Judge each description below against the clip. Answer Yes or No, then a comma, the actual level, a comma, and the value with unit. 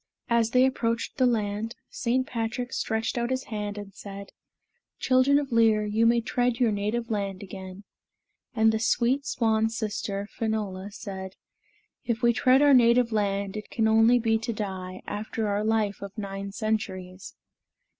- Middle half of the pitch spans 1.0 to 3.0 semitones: Yes, average, 2.7 semitones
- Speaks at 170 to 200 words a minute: No, average, 155 wpm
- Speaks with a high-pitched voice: Yes, high, 220 Hz